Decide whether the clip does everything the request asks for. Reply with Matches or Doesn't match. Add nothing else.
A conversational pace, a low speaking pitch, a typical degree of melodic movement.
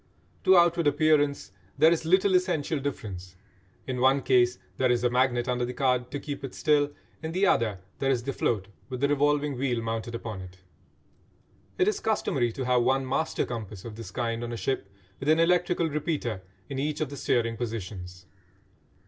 Matches